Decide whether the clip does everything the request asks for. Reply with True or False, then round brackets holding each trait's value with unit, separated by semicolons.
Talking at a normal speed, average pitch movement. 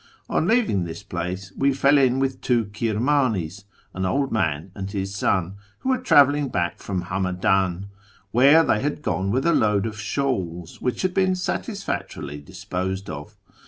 False (170 wpm; 6.9 semitones)